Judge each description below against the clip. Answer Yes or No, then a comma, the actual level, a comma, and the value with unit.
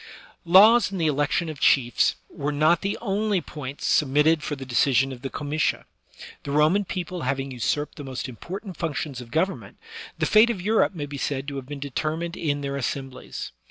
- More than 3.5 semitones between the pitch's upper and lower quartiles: Yes, average, 4.3 semitones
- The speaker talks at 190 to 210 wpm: Yes, average, 195 wpm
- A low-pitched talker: No, medium, 150 Hz